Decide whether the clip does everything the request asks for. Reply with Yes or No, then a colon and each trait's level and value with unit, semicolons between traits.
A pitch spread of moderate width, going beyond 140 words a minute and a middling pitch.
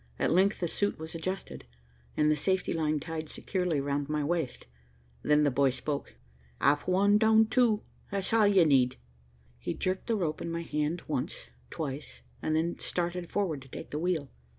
Yes: average, 4.0 semitones; average, 180 wpm; medium, 165 Hz